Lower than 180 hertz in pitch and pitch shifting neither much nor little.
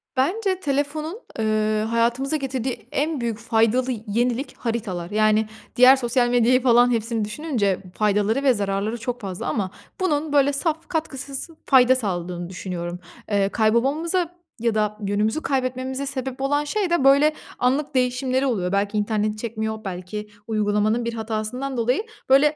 No: high, 240 Hz; average, 4.3 semitones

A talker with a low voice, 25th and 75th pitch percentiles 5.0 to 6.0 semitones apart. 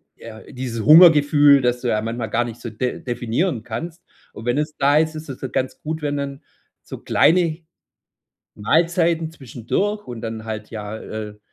Yes: low, 130 Hz; wide, 5.6 semitones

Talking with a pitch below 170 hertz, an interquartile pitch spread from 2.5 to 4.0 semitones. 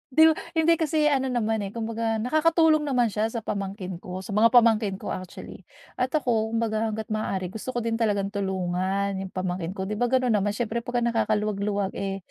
No: high, 220 Hz; average, 3.6 semitones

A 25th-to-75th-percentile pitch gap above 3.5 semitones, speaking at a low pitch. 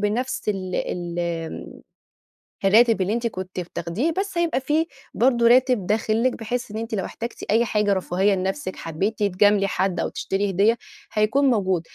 No: average, 4.1 semitones; high, 210 Hz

